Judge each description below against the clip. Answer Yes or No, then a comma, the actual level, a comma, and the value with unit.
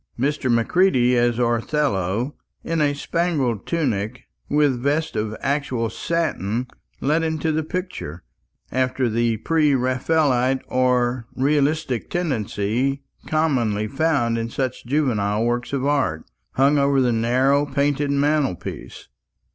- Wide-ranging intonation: No, average, 3.9 semitones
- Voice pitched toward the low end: Yes, low, 130 Hz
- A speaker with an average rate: No, slow, 115 wpm